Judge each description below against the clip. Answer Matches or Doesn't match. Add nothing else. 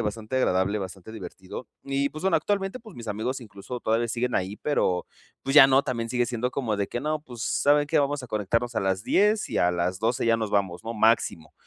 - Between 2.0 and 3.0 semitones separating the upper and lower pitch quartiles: Doesn't match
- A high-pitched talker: Doesn't match